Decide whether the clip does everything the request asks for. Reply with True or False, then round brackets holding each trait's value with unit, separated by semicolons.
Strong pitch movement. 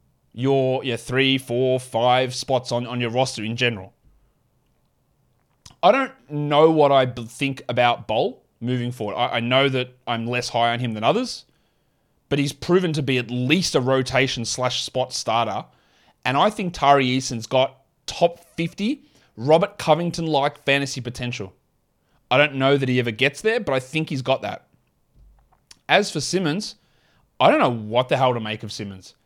False (2.9 semitones)